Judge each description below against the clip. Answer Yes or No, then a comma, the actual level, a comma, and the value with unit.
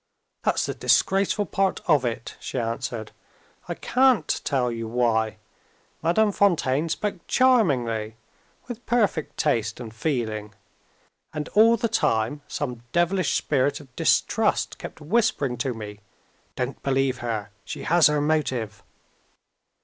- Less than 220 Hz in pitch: Yes, low, 135 Hz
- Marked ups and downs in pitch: Yes, wide, 8.0 semitones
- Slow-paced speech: Yes, slow, 125 wpm